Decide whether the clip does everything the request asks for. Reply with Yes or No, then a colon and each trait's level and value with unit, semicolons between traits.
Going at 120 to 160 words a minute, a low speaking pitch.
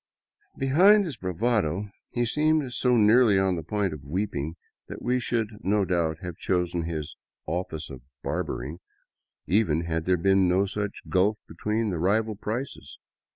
Yes: average, 155 wpm; very low, 95 Hz